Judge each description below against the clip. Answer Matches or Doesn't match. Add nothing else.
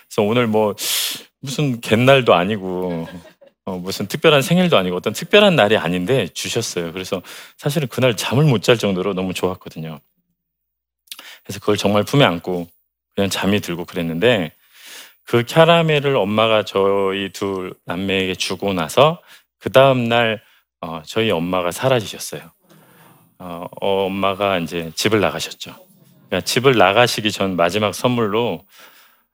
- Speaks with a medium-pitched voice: Doesn't match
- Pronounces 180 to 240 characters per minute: Doesn't match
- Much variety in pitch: Doesn't match